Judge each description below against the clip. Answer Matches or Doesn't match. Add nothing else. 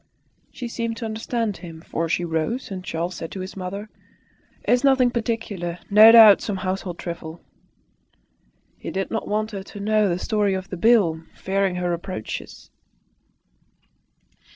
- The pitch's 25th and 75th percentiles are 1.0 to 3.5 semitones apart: Doesn't match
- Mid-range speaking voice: Doesn't match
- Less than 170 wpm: Matches